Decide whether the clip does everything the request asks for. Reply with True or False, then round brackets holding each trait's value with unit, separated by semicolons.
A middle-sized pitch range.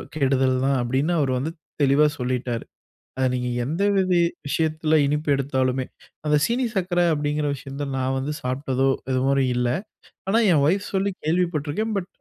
True (3.8 semitones)